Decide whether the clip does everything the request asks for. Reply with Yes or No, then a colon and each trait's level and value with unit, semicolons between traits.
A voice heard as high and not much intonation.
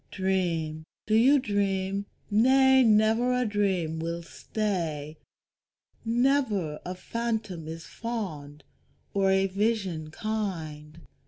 No: high, 195 Hz; average, 5.2 semitones